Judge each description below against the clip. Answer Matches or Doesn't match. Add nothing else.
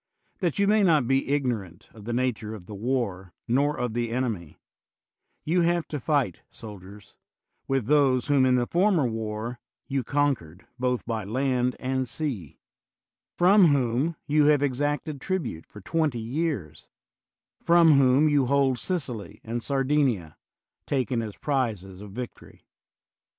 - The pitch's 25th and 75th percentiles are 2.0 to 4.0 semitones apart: Doesn't match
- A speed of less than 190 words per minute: Matches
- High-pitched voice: Doesn't match